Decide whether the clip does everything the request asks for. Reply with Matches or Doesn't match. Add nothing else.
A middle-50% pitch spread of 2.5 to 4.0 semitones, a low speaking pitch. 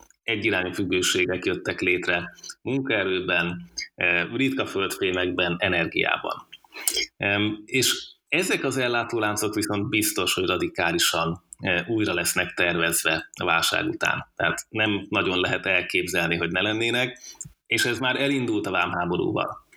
Doesn't match